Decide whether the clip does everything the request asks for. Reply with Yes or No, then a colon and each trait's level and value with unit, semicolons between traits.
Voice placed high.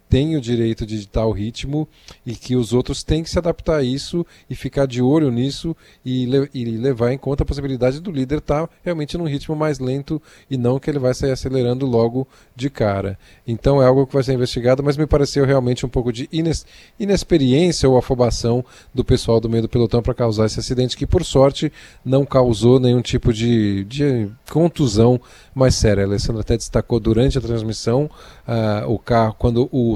No: low, 130 Hz